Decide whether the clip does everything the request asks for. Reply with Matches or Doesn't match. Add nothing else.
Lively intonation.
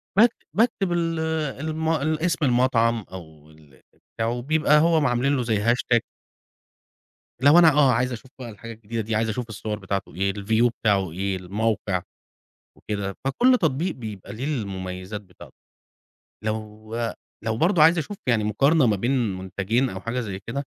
Matches